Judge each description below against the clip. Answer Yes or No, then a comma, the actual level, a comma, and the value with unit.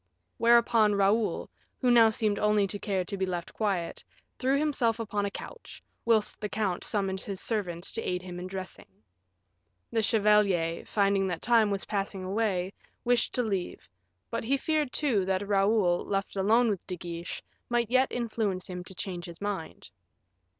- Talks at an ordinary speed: Yes, average, 170 wpm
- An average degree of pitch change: Yes, average, 3.4 semitones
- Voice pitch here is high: Yes, high, 205 Hz